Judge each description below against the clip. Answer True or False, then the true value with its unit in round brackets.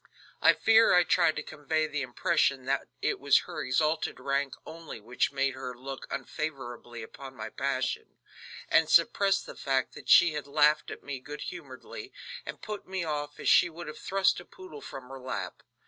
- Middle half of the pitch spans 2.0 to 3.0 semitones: False (3.7 semitones)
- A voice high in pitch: False (145 Hz)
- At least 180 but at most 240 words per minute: True (185 wpm)